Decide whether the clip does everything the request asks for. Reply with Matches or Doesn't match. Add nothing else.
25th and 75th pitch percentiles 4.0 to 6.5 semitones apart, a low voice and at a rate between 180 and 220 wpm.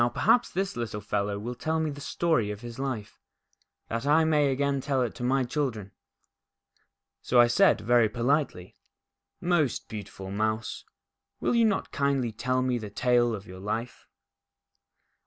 Doesn't match